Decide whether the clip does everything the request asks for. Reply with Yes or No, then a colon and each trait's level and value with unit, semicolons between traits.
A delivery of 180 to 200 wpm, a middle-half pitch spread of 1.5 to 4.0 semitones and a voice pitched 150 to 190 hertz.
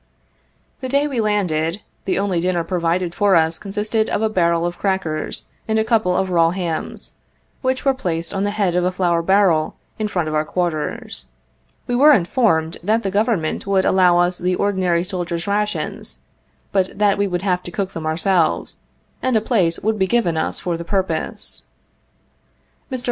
Yes: average, 185 wpm; average, 3.5 semitones; medium, 185 Hz